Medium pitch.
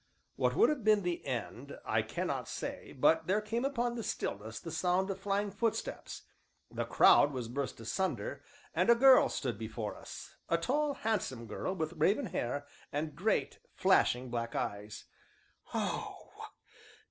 Yes: medium, 165 Hz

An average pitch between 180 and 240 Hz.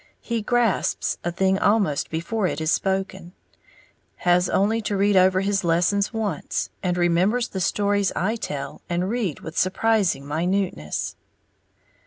Yes: high, 190 Hz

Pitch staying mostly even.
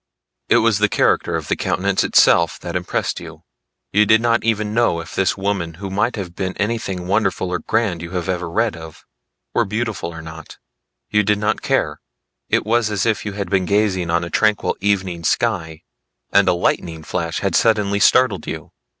No: average, 3.4 semitones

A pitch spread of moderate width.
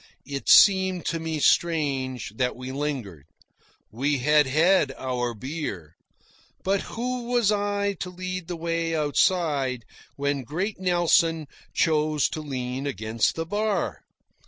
No: wide, 5.7 semitones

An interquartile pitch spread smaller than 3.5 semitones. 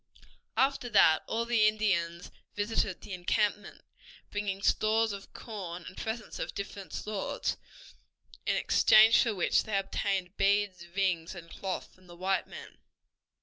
Yes: average, 2.7 semitones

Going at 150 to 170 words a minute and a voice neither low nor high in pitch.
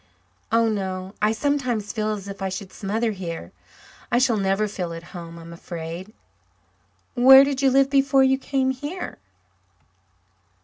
No: average, 160 wpm; high, 215 Hz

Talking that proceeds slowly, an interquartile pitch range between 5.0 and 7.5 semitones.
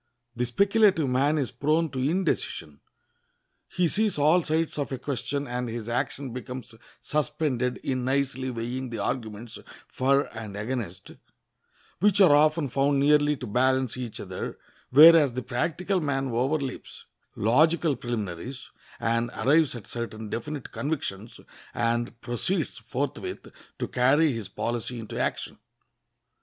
No: slow, 130 wpm; average, 4.0 semitones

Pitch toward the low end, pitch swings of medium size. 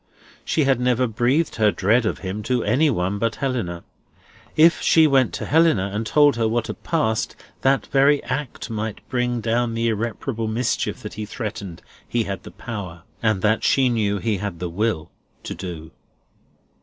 Yes: low, 115 Hz; average, 3.8 semitones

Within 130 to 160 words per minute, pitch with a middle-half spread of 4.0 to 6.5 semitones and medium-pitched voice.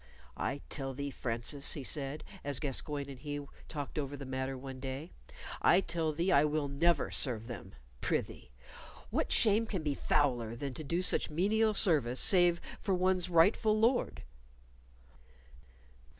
Yes: average, 150 wpm; average, 4.5 semitones; medium, 145 Hz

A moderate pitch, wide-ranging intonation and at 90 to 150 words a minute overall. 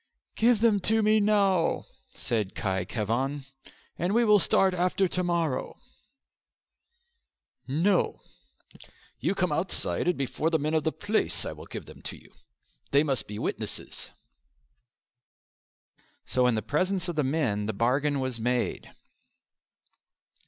Yes: medium, 155 Hz; wide, 6.9 semitones; average, 145 wpm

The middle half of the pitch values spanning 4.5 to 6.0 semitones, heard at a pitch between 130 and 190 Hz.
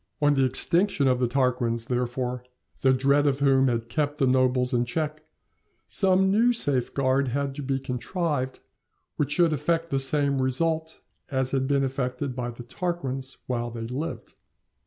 No: average, 2.7 semitones; low, 135 Hz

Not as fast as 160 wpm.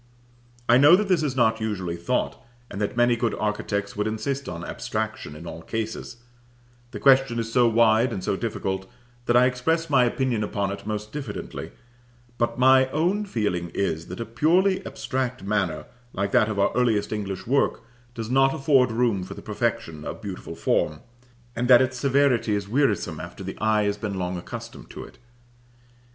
No: average, 180 wpm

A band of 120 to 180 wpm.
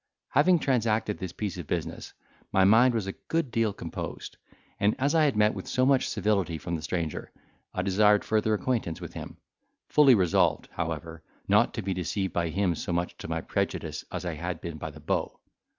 No: average, 200 wpm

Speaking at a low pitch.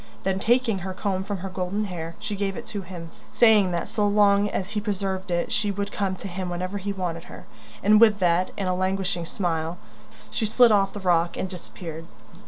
No: high, 190 Hz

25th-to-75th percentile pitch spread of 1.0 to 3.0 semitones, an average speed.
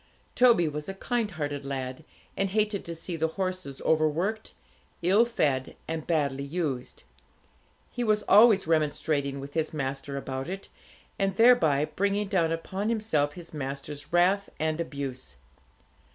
No: wide, 5.5 semitones; average, 145 wpm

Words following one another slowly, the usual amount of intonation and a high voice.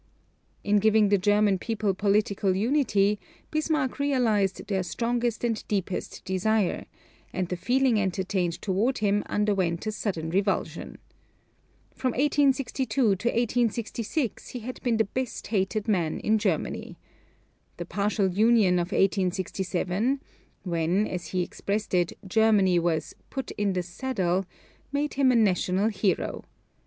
Yes: slow, 130 wpm; average, 3.8 semitones; high, 205 Hz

